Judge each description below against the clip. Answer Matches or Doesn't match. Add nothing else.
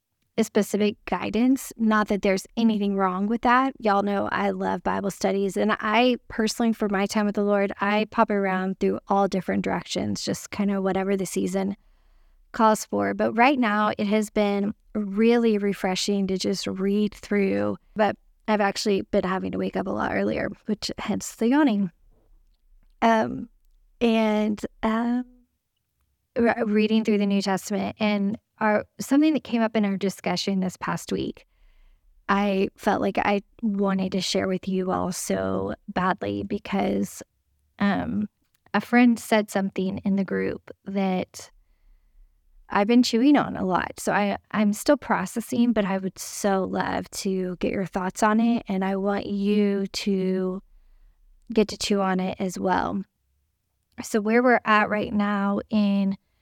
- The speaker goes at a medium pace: Matches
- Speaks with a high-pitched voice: Matches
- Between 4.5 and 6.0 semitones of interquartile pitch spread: Doesn't match